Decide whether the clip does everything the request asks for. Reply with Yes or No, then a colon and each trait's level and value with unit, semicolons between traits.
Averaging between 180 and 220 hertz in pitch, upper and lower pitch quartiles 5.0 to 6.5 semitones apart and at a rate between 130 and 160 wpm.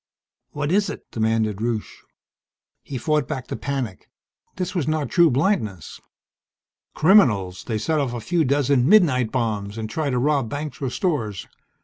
No: low, 135 Hz; wide, 5.6 semitones; average, 155 wpm